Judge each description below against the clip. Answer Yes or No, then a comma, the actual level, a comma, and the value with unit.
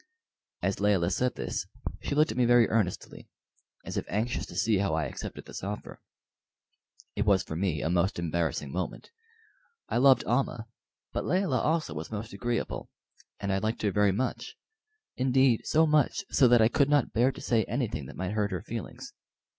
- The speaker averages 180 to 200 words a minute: Yes, average, 185 wpm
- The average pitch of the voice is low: Yes, low, 110 Hz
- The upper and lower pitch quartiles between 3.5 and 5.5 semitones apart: Yes, average, 5.0 semitones